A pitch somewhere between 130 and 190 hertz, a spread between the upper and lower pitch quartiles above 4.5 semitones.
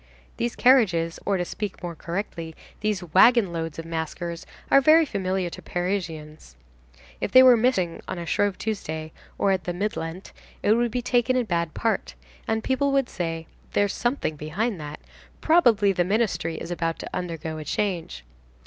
Yes: medium, 185 Hz; wide, 5.4 semitones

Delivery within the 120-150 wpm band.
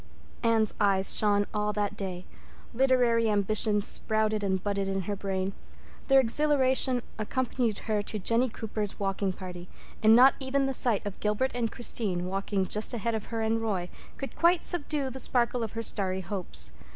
No: average, 170 wpm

